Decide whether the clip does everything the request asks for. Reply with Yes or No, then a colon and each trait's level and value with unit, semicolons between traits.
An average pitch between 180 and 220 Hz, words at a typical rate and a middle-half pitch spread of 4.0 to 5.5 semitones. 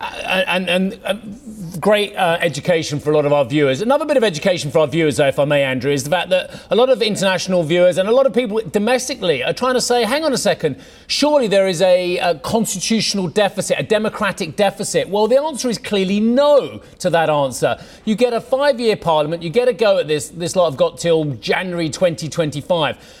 No: high, 190 Hz; fast, 220 wpm; average, 5.2 semitones